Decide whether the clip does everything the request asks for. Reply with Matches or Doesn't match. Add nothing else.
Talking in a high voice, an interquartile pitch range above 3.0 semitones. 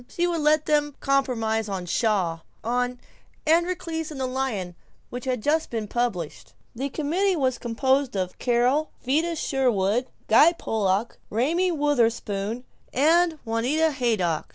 Matches